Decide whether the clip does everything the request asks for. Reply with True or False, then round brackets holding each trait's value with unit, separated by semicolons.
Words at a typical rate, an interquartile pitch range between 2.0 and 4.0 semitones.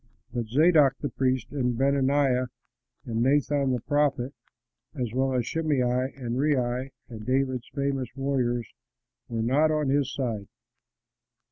False (130 wpm; 2.4 semitones)